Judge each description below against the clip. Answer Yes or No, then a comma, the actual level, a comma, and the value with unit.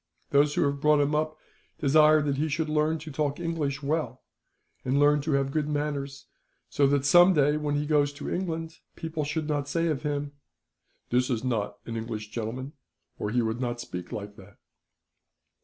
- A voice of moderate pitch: Yes, medium, 145 Hz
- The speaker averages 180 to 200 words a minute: Yes, average, 190 wpm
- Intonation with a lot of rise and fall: No, average, 2.8 semitones